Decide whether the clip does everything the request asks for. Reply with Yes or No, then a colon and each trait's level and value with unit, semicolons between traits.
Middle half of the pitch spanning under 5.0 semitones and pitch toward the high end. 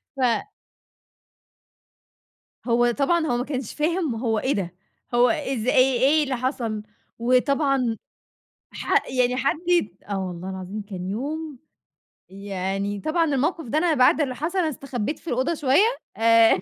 No: average, 5.3 semitones; very high, 255 Hz